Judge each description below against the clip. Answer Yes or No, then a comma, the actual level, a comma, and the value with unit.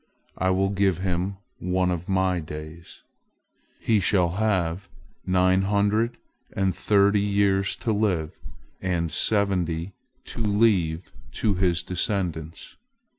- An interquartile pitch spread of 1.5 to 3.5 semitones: Yes, narrow, 2.6 semitones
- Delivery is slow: Yes, slow, 115 wpm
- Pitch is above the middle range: No, very low, 95 Hz